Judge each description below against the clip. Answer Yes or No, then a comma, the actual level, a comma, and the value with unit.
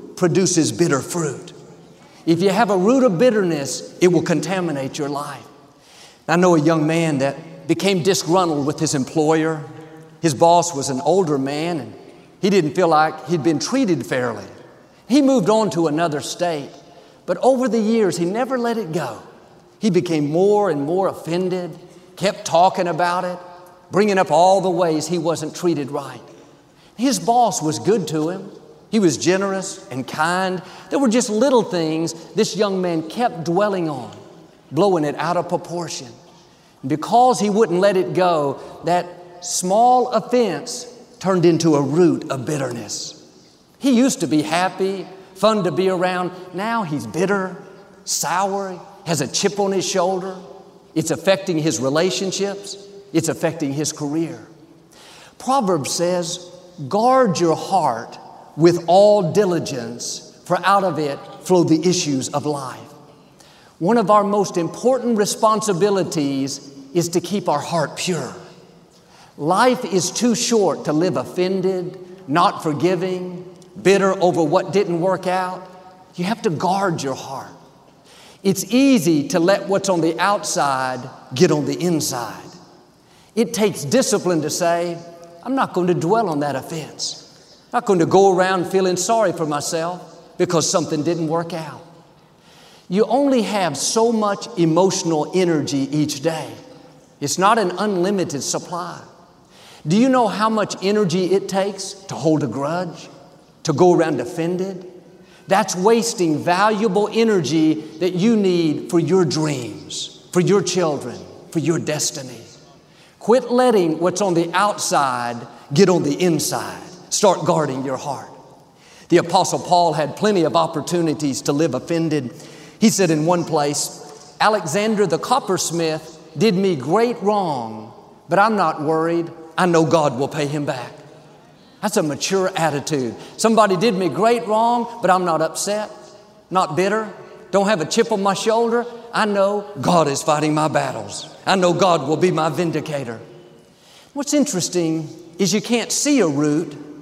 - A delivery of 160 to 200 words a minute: No, average, 150 wpm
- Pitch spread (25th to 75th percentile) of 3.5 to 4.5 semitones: Yes, average, 3.8 semitones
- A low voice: No, medium, 175 Hz